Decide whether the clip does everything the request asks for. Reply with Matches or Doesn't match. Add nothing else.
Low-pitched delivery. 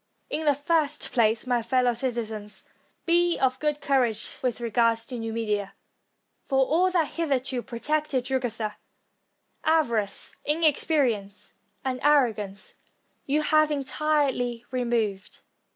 Doesn't match